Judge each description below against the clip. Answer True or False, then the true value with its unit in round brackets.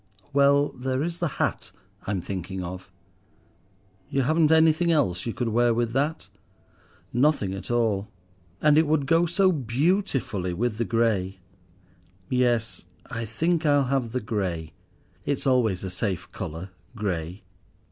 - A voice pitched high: False (120 Hz)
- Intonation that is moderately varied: False (7.1 semitones)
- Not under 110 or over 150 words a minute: True (135 wpm)